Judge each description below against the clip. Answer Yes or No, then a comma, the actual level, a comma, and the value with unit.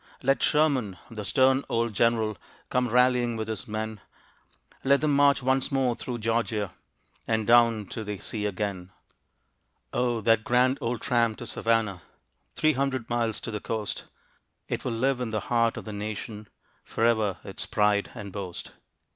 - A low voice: Yes, low, 115 Hz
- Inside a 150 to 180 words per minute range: Yes, average, 160 wpm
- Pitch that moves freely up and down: No, average, 2.8 semitones